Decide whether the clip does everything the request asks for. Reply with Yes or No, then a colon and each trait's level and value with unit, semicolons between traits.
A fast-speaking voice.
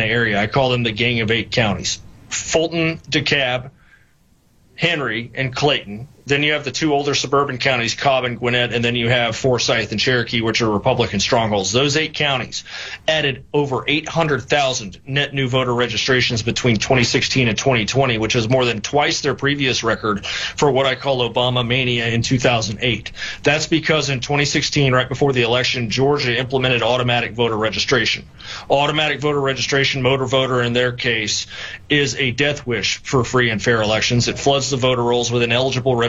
No: average, 175 wpm